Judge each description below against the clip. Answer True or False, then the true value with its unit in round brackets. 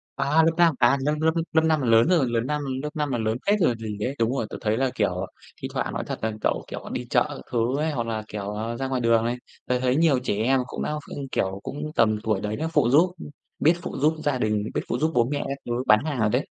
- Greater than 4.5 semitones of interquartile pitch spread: True (4.9 semitones)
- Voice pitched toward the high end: False (125 Hz)